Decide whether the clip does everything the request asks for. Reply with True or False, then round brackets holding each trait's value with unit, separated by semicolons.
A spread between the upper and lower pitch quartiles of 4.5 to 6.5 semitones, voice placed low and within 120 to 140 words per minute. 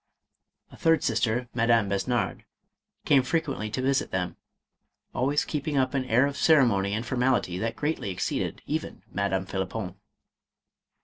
True (5.4 semitones; 120 Hz; 135 wpm)